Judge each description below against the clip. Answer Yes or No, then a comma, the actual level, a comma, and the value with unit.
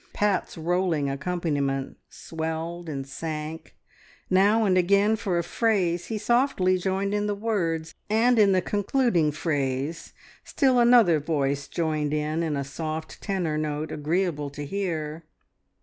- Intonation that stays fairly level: No, average, 4.7 semitones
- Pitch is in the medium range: Yes, medium, 170 Hz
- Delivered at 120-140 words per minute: Yes, slow, 135 wpm